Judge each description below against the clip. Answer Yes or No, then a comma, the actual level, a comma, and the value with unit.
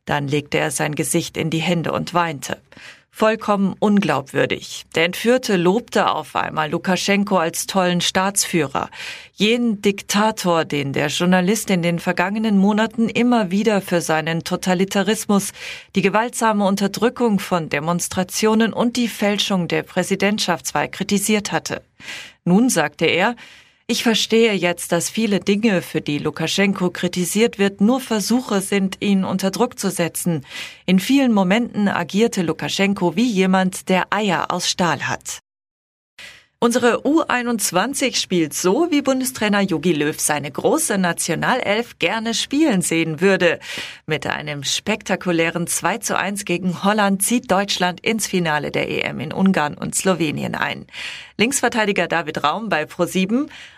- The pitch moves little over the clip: No, average, 4.1 semitones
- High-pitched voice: Yes, high, 195 Hz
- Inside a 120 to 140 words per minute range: Yes, average, 135 wpm